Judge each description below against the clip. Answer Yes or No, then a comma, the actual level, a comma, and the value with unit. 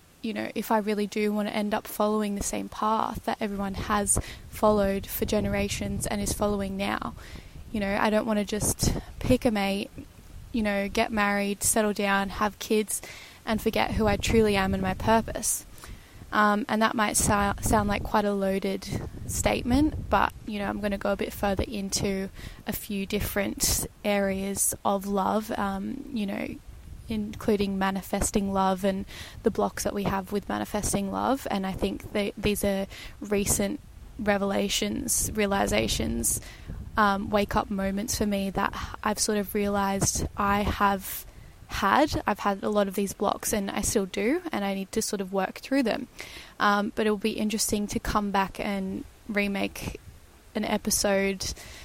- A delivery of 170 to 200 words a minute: Yes, average, 175 wpm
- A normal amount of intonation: No, narrow, 1.5 semitones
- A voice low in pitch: No, high, 205 Hz